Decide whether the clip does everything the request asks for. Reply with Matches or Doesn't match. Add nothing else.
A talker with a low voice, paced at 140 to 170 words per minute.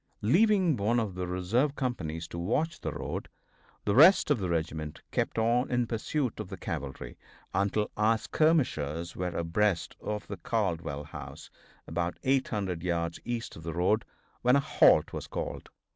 Matches